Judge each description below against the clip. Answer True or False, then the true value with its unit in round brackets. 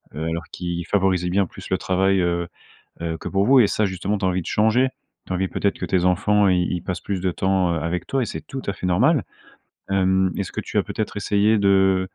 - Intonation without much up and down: True (2.2 semitones)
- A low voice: True (95 Hz)